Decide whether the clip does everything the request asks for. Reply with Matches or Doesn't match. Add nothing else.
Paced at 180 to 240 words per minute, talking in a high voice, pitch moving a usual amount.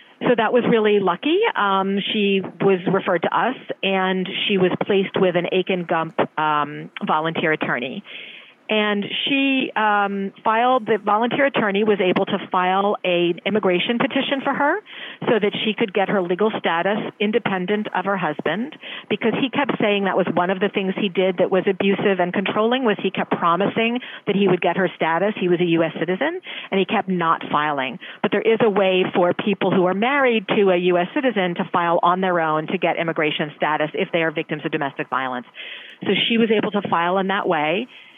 Matches